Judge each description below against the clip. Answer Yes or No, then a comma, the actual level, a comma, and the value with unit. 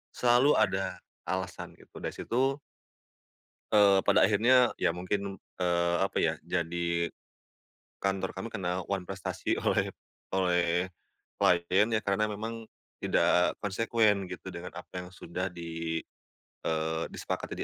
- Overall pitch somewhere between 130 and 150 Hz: No, very low, 95 Hz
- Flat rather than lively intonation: No, average, 3.1 semitones